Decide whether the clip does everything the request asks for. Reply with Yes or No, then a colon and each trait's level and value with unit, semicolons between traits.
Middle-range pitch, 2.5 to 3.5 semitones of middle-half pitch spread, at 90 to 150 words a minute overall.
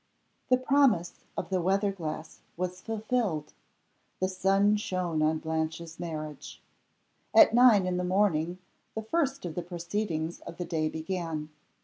No: medium, 180 Hz; average, 4.3 semitones; average, 140 wpm